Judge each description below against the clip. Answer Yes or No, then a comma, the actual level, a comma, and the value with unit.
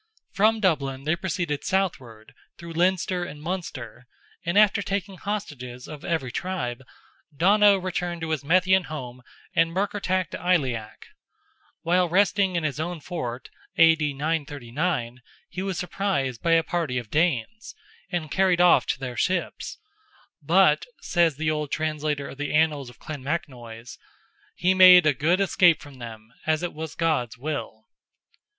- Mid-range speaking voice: Yes, medium, 160 Hz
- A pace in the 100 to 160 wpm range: Yes, average, 145 wpm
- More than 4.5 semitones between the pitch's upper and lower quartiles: Yes, average, 4.9 semitones